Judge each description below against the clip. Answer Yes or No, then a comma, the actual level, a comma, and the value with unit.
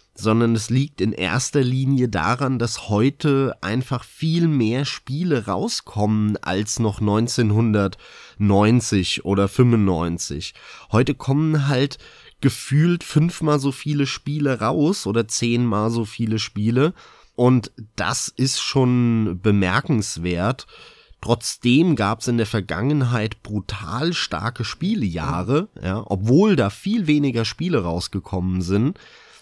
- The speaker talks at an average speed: No, slow, 110 wpm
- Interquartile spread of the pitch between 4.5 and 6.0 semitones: Yes, average, 4.8 semitones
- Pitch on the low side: Yes, low, 115 Hz